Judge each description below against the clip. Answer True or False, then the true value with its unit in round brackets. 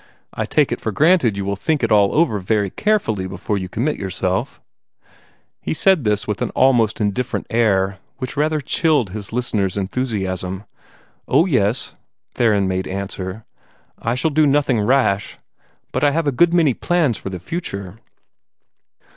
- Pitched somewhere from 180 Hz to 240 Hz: False (110 Hz)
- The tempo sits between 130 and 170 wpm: True (160 wpm)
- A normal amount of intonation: False (6.5 semitones)